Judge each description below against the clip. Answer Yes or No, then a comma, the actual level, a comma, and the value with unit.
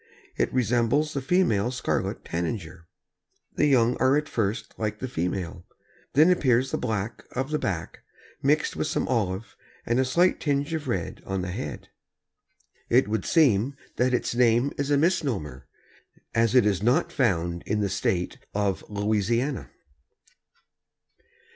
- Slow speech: No, average, 150 wpm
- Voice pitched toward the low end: Yes, low, 115 Hz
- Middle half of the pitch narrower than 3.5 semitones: No, wide, 5.5 semitones